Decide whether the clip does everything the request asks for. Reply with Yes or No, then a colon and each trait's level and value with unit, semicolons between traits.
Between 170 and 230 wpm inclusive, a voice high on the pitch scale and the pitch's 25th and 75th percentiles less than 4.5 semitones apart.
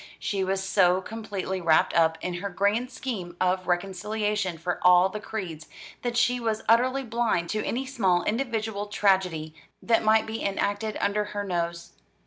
No: average, 160 wpm; high, 200 Hz; average, 3.6 semitones